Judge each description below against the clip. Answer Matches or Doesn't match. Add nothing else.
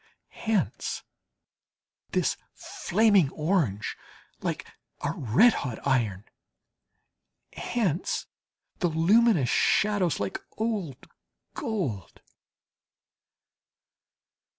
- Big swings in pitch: Matches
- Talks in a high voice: Doesn't match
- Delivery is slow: Matches